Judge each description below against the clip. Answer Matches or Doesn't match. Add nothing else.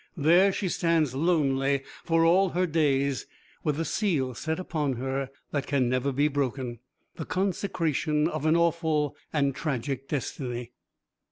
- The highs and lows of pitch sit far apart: Doesn't match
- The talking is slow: Doesn't match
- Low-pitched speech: Doesn't match